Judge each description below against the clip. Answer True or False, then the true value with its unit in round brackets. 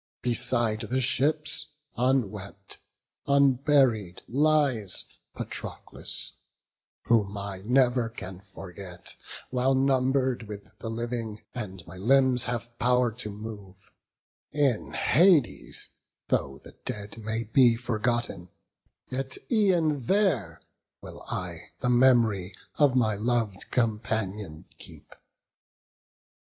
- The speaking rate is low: True (100 wpm)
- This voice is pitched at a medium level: False (120 Hz)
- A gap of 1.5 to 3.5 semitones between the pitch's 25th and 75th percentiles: False (4.4 semitones)